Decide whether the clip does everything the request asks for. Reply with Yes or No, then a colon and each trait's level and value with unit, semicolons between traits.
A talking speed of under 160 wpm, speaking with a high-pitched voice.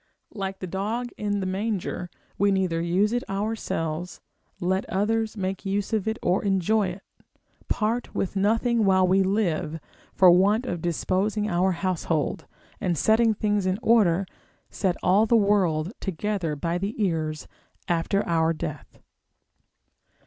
Yes: average, 140 wpm; high, 195 Hz